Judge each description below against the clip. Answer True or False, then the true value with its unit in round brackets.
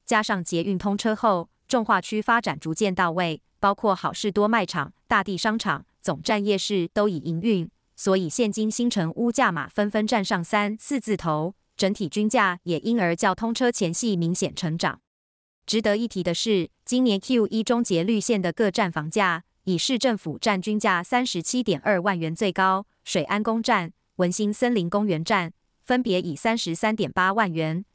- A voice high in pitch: True (205 Hz)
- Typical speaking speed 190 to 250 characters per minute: False (270 characters per minute)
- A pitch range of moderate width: True (3.8 semitones)